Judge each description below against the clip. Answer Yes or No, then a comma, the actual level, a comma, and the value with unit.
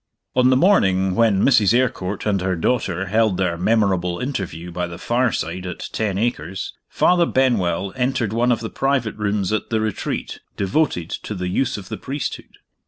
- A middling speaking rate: Yes, average, 170 wpm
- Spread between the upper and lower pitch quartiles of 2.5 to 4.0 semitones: No, average, 4.8 semitones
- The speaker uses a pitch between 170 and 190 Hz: No, low, 105 Hz